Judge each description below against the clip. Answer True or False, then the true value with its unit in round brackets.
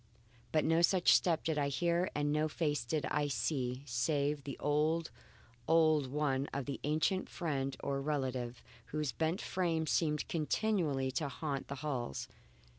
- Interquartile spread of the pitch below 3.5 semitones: True (2.7 semitones)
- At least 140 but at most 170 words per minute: True (155 wpm)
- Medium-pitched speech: True (150 Hz)